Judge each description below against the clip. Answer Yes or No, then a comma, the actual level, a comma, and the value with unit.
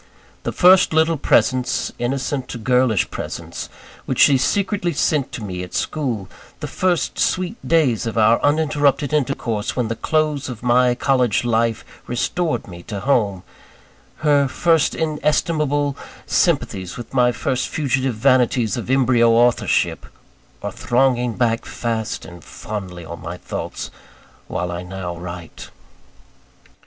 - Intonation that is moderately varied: Yes, average, 4.7 semitones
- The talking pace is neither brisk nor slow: No, slow, 130 wpm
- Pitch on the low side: Yes, low, 125 Hz